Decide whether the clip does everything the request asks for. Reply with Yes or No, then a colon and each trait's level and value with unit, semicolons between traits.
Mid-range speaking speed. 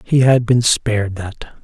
Yes: average, 185 wpm